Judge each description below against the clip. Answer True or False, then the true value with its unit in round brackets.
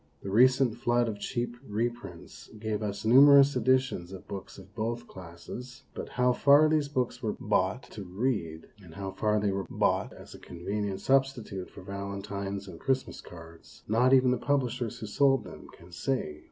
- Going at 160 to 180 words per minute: True (175 wpm)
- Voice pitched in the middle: False (110 Hz)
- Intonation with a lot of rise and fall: False (4.7 semitones)